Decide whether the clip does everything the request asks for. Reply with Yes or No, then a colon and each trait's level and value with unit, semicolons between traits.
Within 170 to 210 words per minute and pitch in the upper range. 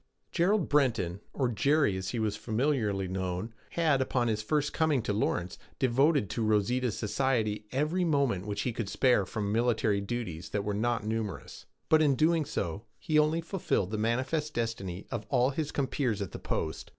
No: average, 175 wpm; low, 120 Hz